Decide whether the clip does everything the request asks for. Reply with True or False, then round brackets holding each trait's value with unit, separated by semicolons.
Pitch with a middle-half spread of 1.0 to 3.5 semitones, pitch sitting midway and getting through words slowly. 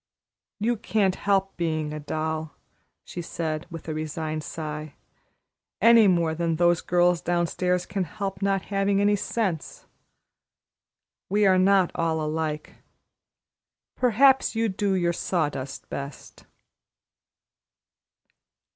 False (3.9 semitones; 175 Hz; 110 wpm)